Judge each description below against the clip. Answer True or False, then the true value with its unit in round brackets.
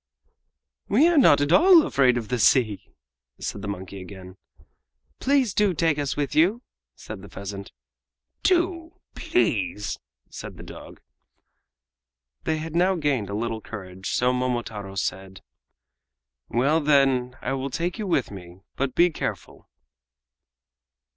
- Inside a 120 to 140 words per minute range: True (135 wpm)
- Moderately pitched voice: False (130 Hz)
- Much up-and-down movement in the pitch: True (9.0 semitones)